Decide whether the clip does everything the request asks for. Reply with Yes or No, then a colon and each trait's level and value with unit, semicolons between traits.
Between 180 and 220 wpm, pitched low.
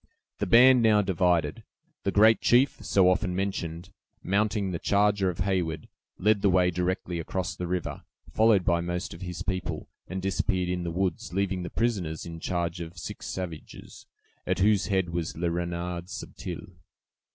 No: average, 165 wpm; very low, 90 Hz